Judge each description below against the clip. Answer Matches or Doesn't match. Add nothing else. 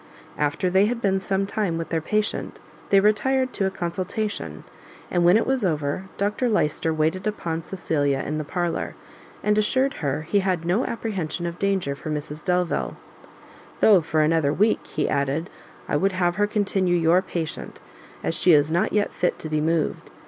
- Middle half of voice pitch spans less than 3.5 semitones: Doesn't match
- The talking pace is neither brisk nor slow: Matches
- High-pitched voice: Doesn't match